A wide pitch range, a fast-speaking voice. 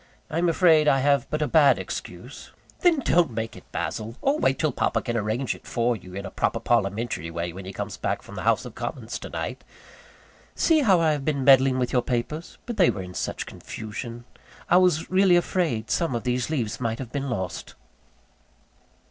Yes: wide, 6.2 semitones; fast, 210 wpm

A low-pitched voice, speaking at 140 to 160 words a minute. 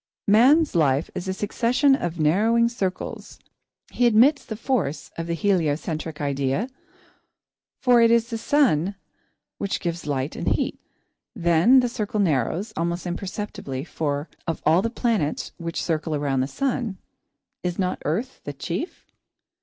No: medium, 180 Hz; average, 155 wpm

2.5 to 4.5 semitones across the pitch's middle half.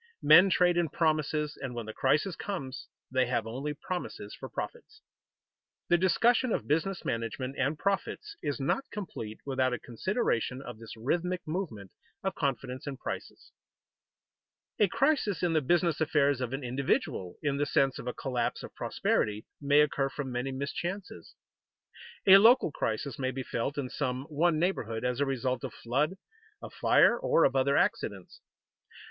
No: wide, 5.4 semitones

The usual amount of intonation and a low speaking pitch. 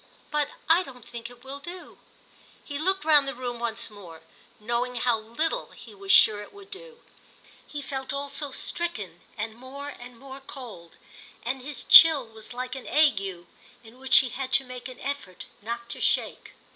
No: average, 3.9 semitones; very high, 255 Hz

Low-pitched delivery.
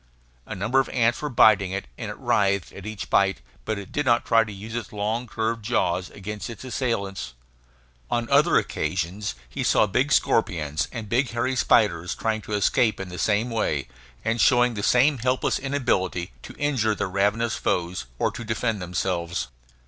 Yes: low, 110 Hz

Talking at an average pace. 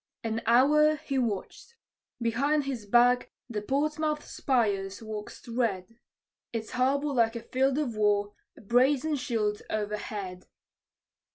No: slow, 120 wpm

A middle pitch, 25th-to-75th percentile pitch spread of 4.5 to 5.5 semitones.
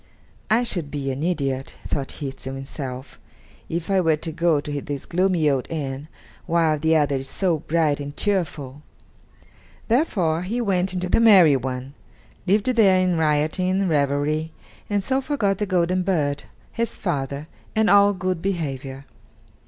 Yes: medium, 160 Hz; average, 4.8 semitones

